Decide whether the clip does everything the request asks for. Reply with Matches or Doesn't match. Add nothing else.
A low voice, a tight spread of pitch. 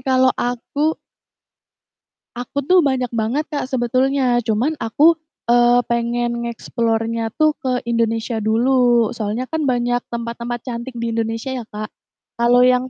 Doesn't match